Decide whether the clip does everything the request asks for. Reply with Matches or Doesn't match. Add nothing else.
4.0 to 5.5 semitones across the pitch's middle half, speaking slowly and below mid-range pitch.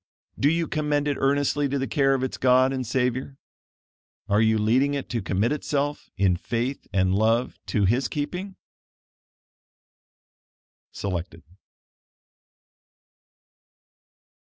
Matches